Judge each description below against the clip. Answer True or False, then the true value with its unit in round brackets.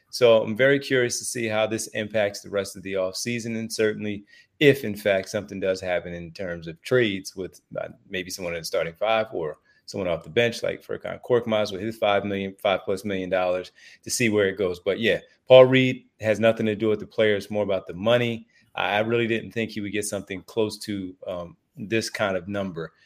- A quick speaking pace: True (225 wpm)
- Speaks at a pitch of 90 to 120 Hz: True (105 Hz)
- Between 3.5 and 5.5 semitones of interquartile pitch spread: False (2.8 semitones)